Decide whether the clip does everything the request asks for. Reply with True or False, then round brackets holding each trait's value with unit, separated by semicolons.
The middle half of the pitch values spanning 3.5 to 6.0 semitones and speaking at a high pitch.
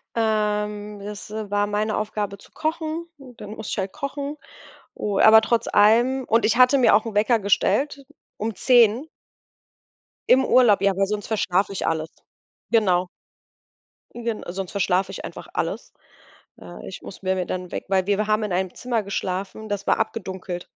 False (2.9 semitones; 210 Hz)